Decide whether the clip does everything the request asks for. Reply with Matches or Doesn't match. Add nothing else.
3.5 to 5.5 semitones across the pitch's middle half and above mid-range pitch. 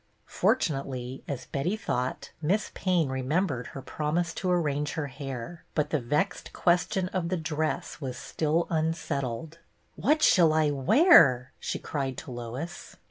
Doesn't match